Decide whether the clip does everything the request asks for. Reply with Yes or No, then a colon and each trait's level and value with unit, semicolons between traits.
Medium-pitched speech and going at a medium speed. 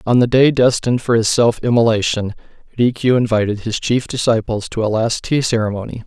No: low, 115 Hz; average, 180 wpm